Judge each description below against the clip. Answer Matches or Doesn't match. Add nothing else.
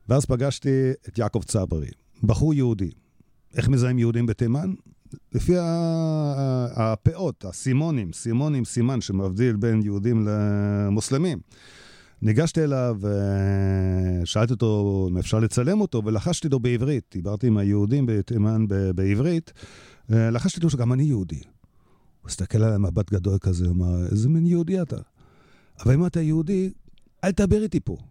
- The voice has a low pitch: Matches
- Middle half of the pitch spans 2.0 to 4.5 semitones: Doesn't match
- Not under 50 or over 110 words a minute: Doesn't match